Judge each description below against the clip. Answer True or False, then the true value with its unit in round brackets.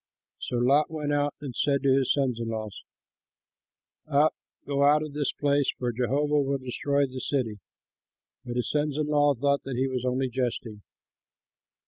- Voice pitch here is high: False (140 Hz)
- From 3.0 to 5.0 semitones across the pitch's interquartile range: False (2.5 semitones)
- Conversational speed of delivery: True (165 wpm)